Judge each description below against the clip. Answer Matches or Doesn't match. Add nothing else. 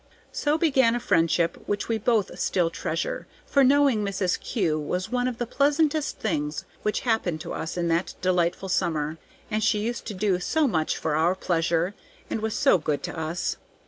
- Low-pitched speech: Doesn't match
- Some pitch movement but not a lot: Doesn't match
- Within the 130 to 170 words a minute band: Doesn't match